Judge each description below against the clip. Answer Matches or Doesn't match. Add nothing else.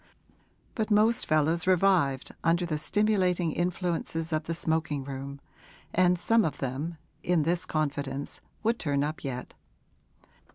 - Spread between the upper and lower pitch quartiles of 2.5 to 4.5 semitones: Matches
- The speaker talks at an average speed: Doesn't match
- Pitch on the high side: Doesn't match